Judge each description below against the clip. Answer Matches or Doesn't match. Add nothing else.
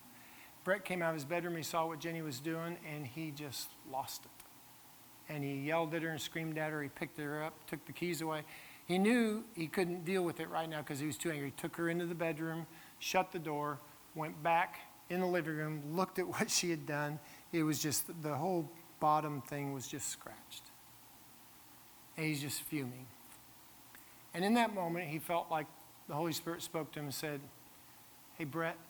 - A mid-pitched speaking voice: Matches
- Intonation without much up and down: Matches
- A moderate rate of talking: Doesn't match